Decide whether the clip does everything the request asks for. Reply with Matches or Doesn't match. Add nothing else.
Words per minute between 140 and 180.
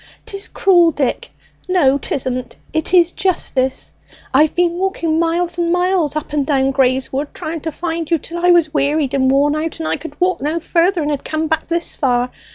Doesn't match